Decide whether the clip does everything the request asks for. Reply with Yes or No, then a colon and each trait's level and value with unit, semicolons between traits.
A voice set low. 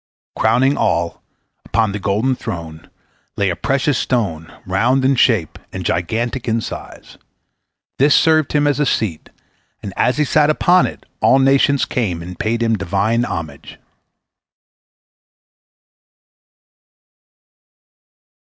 Yes: low, 115 Hz